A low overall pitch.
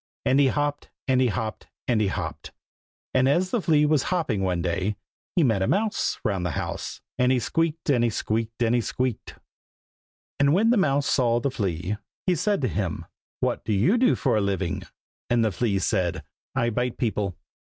Yes: low, 120 Hz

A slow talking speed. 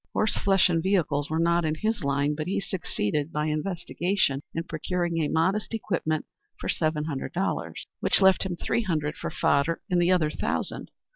No: average, 185 wpm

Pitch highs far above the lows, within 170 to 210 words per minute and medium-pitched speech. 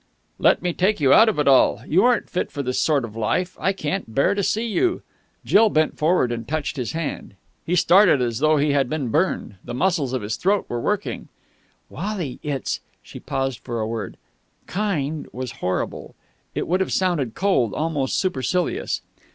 Yes: wide, 6.6 semitones; average, 190 wpm; medium, 150 Hz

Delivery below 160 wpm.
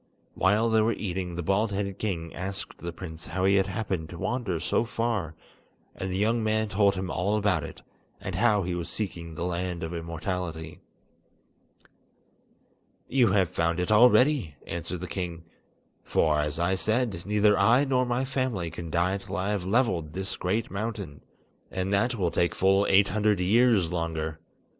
No: average, 175 wpm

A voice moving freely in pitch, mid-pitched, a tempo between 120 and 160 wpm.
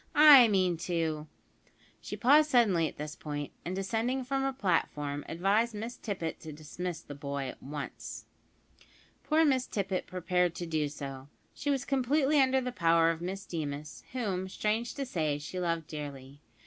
No: wide, 8.0 semitones; medium, 180 Hz; average, 170 wpm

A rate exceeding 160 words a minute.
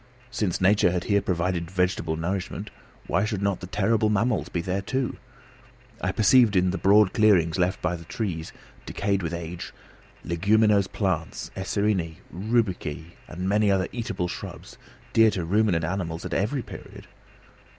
No: average, 150 wpm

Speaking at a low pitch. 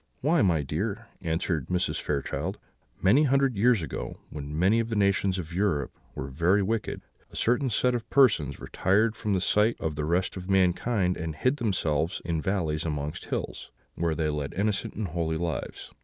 Yes: very low, 90 Hz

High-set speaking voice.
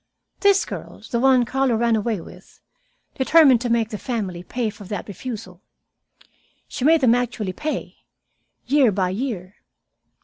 Yes: high, 235 Hz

